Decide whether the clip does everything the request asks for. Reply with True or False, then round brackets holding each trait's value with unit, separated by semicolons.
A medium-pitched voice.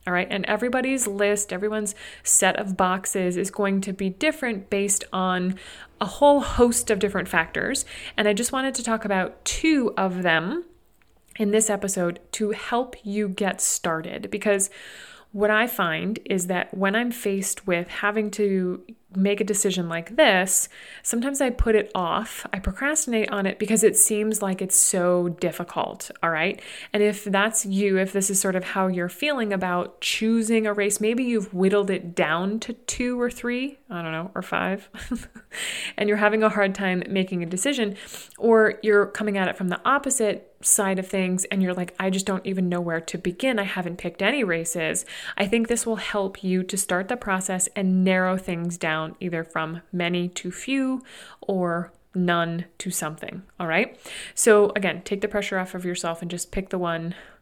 False (195 Hz)